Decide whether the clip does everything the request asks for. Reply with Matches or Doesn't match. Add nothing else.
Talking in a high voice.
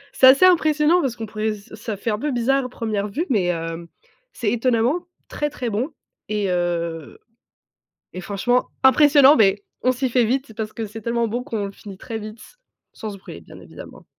Matches